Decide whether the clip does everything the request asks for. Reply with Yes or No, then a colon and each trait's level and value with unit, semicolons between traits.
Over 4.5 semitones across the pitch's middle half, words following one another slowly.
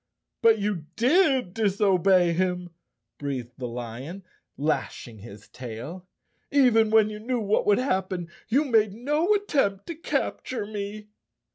No: average, 5.2 semitones; average, 145 wpm